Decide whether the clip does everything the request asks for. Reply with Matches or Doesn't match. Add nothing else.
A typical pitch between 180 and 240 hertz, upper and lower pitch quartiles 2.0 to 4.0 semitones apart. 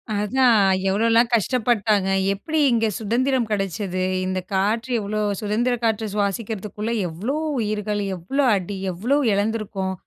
Matches